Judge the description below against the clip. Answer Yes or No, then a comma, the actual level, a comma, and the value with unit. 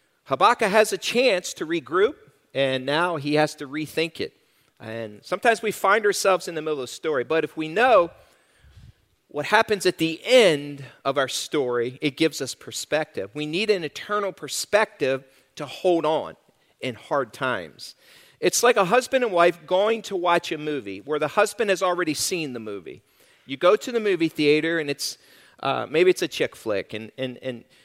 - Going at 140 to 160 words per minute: No, average, 185 wpm